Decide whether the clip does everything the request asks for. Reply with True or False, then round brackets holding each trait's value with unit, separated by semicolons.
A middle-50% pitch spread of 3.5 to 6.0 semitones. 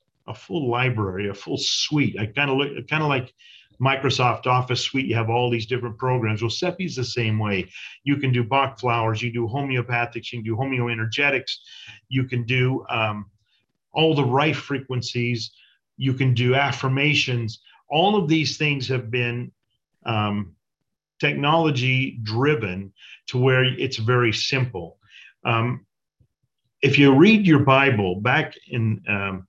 False (3.1 semitones)